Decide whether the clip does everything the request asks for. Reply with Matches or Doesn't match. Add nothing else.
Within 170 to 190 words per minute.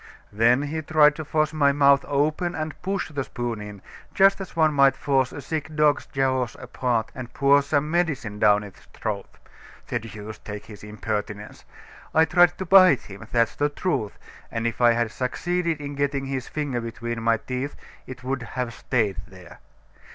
Matches